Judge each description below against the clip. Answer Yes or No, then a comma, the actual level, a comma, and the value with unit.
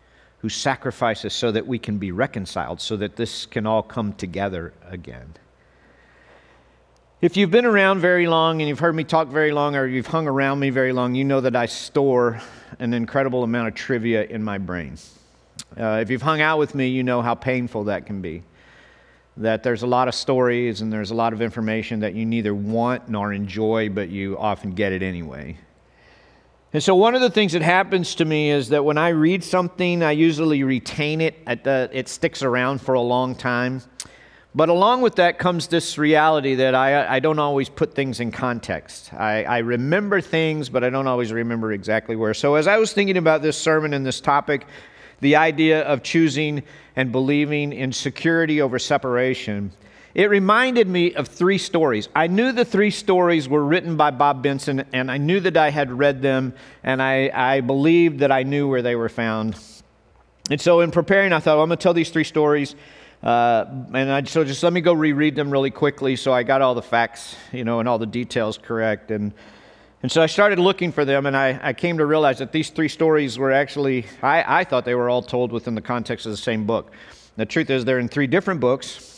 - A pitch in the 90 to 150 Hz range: Yes, low, 135 Hz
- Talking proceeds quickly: Yes, fast, 210 wpm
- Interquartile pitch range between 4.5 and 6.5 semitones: Yes, average, 5.1 semitones